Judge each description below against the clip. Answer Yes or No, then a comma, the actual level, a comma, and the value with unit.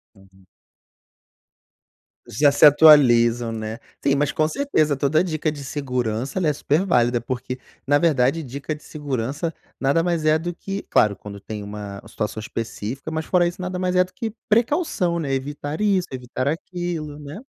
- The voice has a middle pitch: Yes, medium, 145 Hz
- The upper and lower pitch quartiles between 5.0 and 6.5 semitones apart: Yes, wide, 5.5 semitones